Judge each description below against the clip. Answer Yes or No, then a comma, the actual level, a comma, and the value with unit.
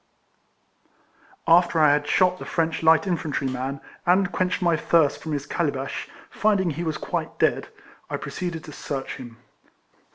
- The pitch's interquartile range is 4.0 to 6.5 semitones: No, average, 3.6 semitones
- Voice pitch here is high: No, medium, 160 Hz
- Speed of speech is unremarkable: Yes, average, 160 wpm